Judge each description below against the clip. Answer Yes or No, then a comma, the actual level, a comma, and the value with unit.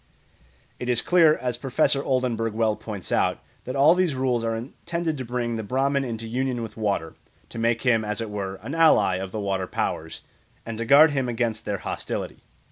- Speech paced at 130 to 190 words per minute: No, average, 200 wpm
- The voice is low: Yes, low, 120 Hz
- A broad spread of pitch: No, average, 3.5 semitones